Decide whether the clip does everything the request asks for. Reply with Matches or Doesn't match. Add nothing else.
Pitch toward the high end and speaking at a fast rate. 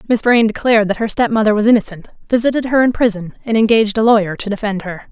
Matches